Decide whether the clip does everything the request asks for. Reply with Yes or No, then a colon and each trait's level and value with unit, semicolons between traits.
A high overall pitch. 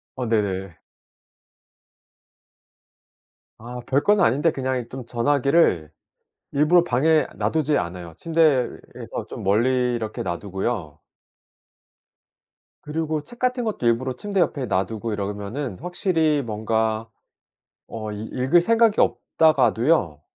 No: low, 125 Hz